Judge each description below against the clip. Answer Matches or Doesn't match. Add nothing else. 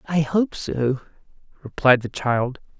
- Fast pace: Doesn't match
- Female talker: Doesn't match